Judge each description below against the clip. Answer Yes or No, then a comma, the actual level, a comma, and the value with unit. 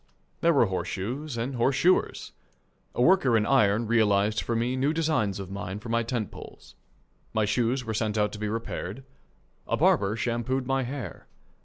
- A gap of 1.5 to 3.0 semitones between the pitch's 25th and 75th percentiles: No, average, 3.8 semitones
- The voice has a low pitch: Yes, low, 115 Hz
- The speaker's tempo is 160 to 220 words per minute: Yes, average, 170 wpm